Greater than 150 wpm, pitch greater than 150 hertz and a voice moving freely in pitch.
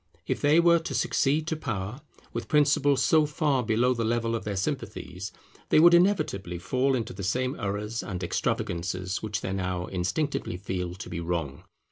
No: average, 175 wpm; low, 110 Hz; wide, 7.6 semitones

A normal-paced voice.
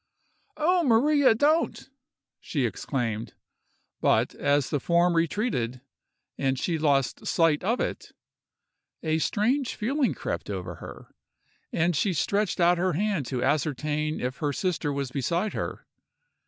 No: slow, 130 wpm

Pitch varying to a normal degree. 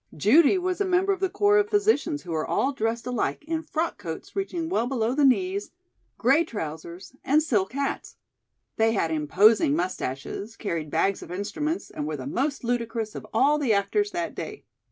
No: wide, 8.9 semitones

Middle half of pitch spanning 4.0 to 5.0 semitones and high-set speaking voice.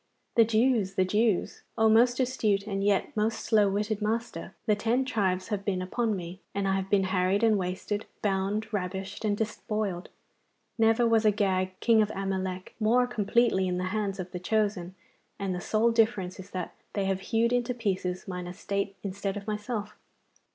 No: average, 2.7 semitones; high, 205 Hz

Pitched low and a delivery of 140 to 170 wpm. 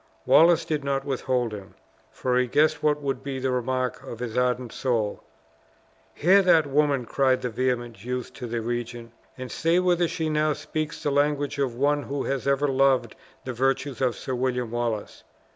No: low, 130 Hz; average, 180 wpm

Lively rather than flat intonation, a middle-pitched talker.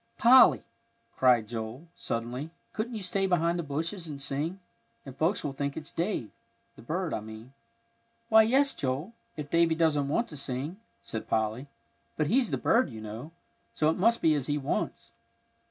Yes: wide, 5.8 semitones; medium, 150 Hz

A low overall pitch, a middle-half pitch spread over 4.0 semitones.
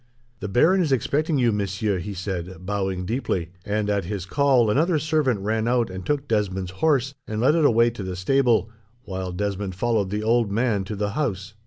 Yes: low, 105 Hz; average, 4.8 semitones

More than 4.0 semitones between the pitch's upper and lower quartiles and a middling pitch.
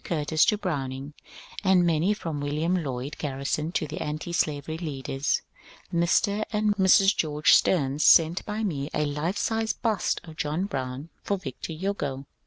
Yes: average, 4.6 semitones; medium, 160 Hz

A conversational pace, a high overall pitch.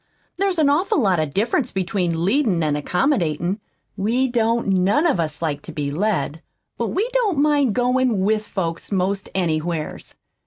Yes: average, 160 wpm; high, 195 Hz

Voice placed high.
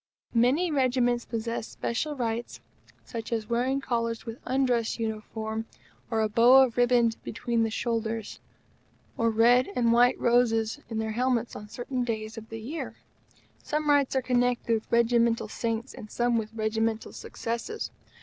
Yes: high, 235 Hz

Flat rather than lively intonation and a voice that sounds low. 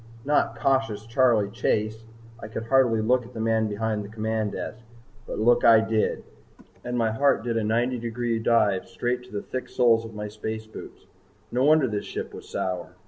Yes: narrow, 2.0 semitones; low, 115 Hz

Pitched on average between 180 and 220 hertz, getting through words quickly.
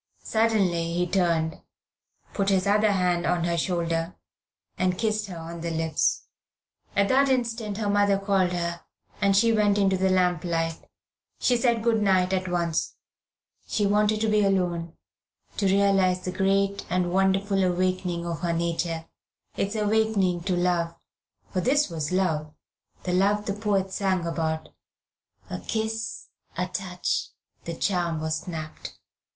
No: medium, 185 Hz; average, 150 wpm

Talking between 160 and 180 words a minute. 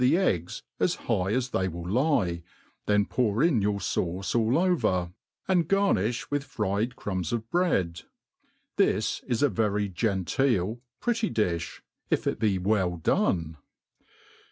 No: average, 140 wpm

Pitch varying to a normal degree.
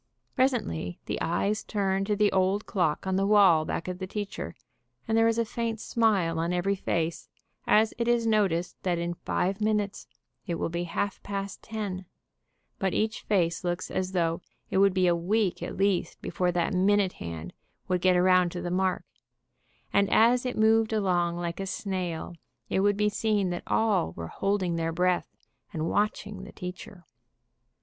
Yes: average, 3.1 semitones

